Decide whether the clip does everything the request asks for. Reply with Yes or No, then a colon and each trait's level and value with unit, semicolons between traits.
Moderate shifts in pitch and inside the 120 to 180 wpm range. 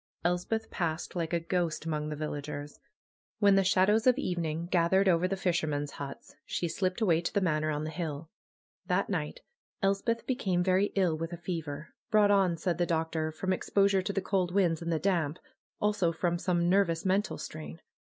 No: average, 3.3 semitones; average, 190 wpm